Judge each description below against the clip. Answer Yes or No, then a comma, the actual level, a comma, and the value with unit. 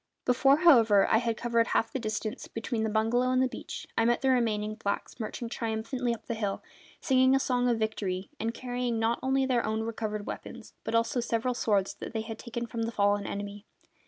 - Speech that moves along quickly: Yes, fast, 210 wpm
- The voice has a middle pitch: No, high, 230 Hz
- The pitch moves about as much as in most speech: No, narrow, 2.2 semitones